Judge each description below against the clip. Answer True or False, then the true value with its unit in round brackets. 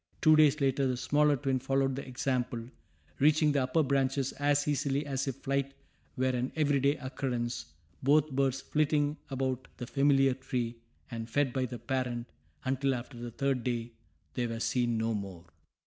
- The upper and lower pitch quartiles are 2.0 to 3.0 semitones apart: True (2.4 semitones)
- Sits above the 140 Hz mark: False (135 Hz)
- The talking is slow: False (170 wpm)